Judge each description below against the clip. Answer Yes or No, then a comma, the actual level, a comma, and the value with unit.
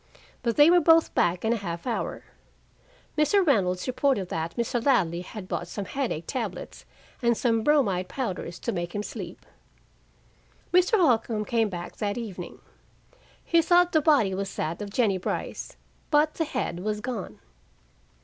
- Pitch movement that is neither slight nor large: No, wide, 7.2 semitones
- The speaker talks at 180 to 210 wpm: No, average, 160 wpm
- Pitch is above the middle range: Yes, high, 225 Hz